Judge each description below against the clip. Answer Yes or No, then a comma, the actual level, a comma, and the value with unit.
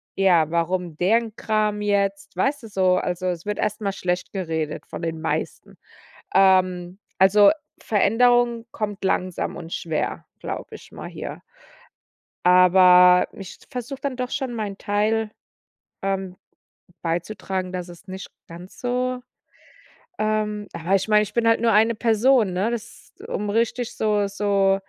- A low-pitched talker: No, high, 200 Hz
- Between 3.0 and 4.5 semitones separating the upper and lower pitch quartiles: Yes, average, 3.3 semitones